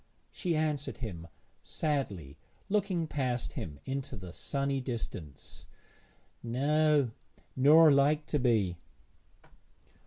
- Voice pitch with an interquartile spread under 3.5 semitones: No, wide, 5.4 semitones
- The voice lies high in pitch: No, medium, 140 Hz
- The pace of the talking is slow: Yes, slow, 95 wpm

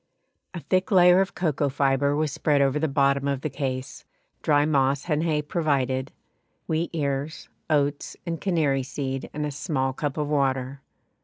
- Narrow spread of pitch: Yes, narrow, 2.3 semitones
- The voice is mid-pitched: Yes, medium, 145 Hz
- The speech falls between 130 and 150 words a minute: No, average, 165 wpm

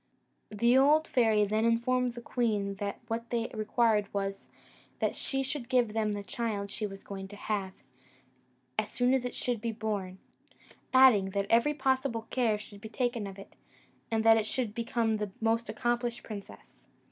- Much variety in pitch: No, average, 2.7 semitones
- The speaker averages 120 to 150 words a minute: No, average, 175 wpm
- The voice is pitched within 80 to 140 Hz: No, high, 225 Hz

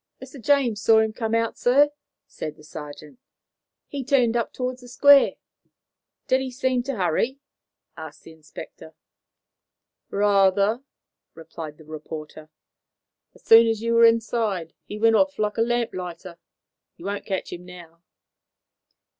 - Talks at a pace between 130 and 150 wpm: Yes, average, 140 wpm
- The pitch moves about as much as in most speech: No, wide, 6.5 semitones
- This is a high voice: Yes, high, 220 Hz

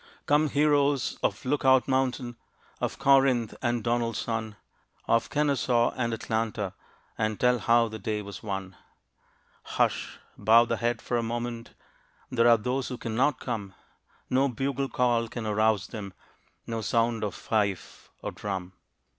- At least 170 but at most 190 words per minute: No, average, 145 wpm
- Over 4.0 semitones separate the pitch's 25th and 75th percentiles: No, average, 2.7 semitones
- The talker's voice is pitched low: Yes, low, 115 Hz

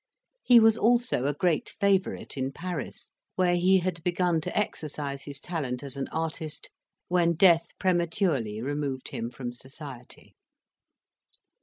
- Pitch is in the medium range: Yes, medium, 160 Hz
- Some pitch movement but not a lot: Yes, average, 4.8 semitones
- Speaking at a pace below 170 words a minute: Yes, slow, 135 wpm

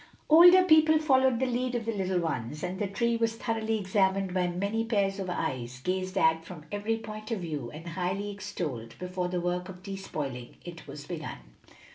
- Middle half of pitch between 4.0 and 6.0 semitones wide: Yes, average, 4.6 semitones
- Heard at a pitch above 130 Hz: Yes, high, 190 Hz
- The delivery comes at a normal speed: Yes, average, 190 wpm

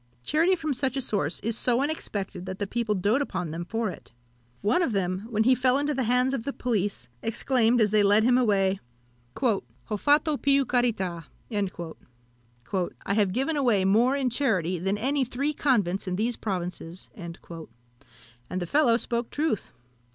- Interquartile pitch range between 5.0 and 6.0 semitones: Yes, average, 5.3 semitones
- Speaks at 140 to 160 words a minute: No, average, 170 wpm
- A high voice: Yes, high, 230 Hz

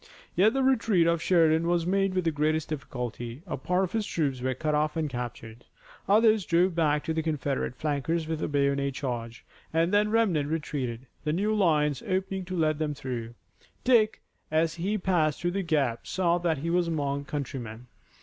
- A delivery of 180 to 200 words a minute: Yes, average, 190 wpm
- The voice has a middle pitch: Yes, medium, 160 Hz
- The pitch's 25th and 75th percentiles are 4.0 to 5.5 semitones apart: Yes, average, 4.4 semitones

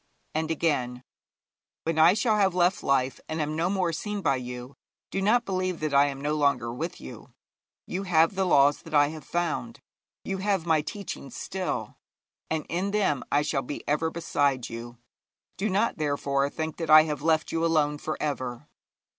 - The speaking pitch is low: No, medium, 155 Hz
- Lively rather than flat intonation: No, average, 4.2 semitones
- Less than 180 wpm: No, average, 185 wpm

